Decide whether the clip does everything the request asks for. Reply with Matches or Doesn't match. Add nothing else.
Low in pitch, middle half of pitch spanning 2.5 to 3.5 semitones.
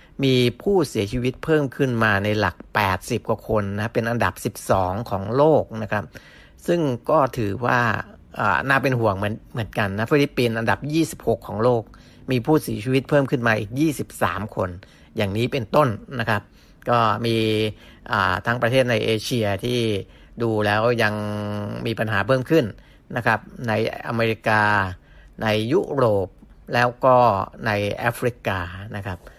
Matches